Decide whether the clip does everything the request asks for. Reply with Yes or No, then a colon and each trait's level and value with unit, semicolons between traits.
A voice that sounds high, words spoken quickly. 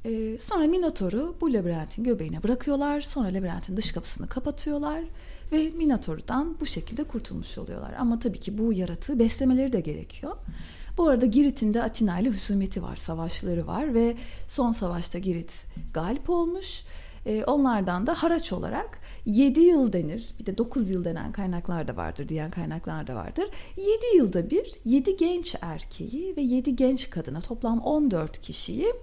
Yes: high, 235 Hz; fast, 150 wpm